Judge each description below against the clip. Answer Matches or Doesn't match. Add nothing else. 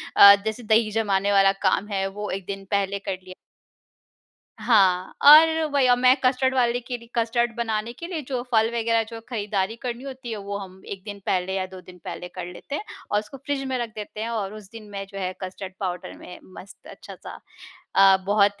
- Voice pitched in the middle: Doesn't match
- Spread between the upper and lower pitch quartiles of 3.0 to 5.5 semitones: Matches